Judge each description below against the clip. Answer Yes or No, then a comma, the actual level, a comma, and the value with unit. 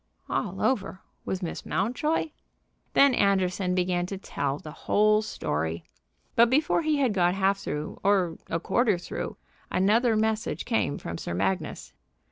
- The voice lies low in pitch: No, high, 195 Hz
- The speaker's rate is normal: Yes, average, 145 wpm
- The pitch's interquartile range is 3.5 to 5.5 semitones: Yes, average, 4.5 semitones